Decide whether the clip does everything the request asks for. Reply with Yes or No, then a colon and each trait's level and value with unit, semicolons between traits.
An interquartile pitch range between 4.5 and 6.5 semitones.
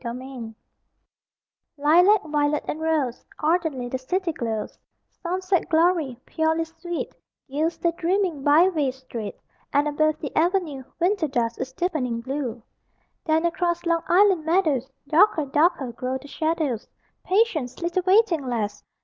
Yes: average, 4.8 semitones